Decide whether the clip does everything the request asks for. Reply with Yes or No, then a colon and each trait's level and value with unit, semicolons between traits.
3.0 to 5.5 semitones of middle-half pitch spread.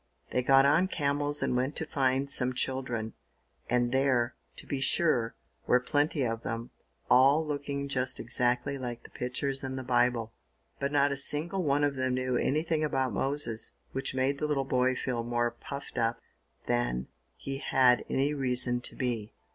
No: narrow, 2.4 semitones